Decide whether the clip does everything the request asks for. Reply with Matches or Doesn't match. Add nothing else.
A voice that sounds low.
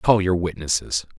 Matches